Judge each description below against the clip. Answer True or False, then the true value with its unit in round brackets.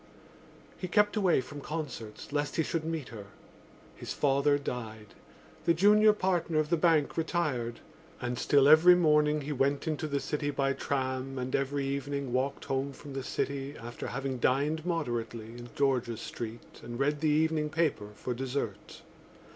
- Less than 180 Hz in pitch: True (140 Hz)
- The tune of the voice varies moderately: True (3.4 semitones)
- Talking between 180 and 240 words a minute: False (165 wpm)